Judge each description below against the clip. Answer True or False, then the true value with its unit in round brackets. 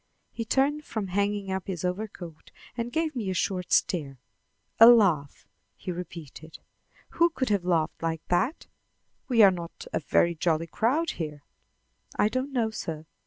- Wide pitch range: True (5.8 semitones)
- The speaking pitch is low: False (190 Hz)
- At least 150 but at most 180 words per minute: True (160 wpm)